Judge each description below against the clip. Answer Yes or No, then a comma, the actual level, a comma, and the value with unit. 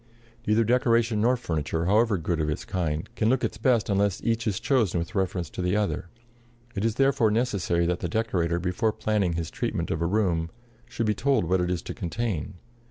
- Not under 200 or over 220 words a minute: Yes, fast, 205 wpm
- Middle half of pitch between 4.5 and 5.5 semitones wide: Yes, average, 4.8 semitones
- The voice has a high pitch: No, low, 100 Hz